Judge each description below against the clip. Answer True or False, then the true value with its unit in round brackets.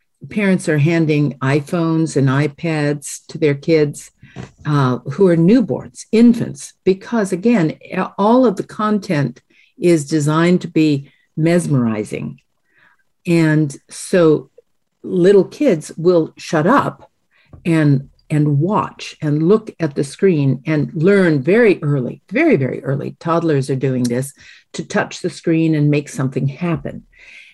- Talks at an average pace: False (130 wpm)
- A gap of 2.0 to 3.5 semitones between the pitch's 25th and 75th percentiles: False (3.9 semitones)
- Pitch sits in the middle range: True (160 Hz)